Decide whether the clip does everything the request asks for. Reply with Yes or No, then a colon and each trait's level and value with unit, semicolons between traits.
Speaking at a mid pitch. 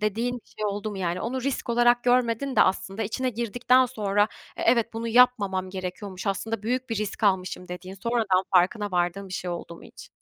No: high, 210 Hz